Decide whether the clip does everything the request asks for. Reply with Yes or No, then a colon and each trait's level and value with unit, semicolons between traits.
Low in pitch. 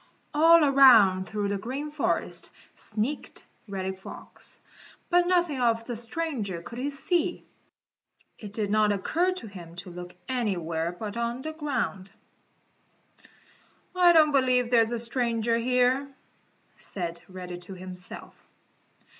No: high, 230 Hz